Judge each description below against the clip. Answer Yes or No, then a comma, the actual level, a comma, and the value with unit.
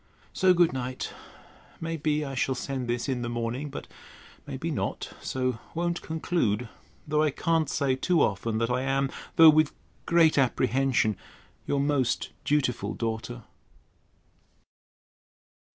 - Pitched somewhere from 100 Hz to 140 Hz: Yes, low, 135 Hz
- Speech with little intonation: No, average, 4.2 semitones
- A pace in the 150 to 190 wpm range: No, slow, 135 wpm